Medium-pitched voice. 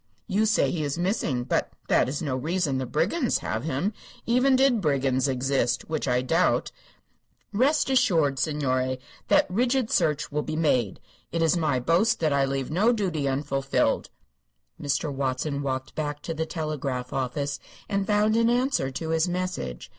Yes: medium, 155 Hz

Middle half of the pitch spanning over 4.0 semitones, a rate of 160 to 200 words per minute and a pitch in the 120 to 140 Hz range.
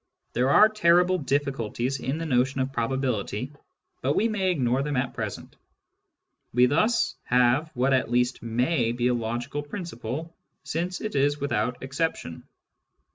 No: average, 4.7 semitones; average, 145 wpm; low, 135 Hz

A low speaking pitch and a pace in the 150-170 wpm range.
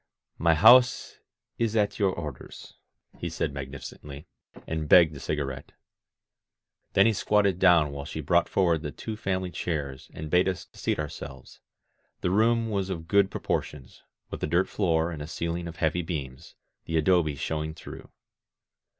Yes: very low, 85 Hz; average, 160 wpm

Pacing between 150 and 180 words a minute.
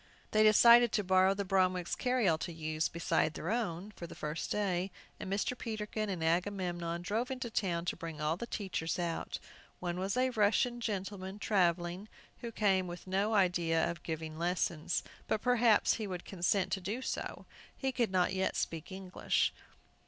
Yes: average, 175 wpm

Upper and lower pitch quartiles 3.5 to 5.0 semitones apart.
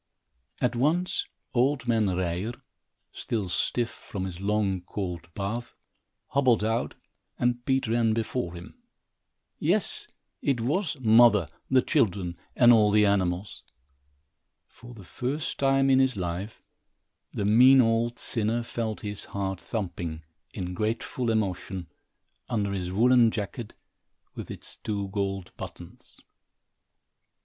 Yes: average, 3.9 semitones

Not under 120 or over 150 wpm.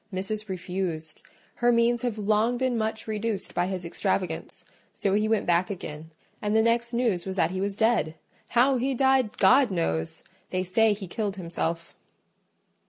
No: average, 165 wpm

